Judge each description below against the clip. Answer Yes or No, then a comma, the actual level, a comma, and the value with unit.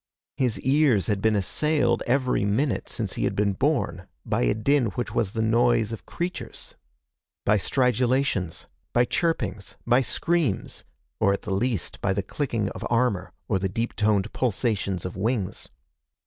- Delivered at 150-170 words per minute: Yes, average, 160 wpm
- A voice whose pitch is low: Yes, low, 115 Hz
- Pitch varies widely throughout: No, average, 4.3 semitones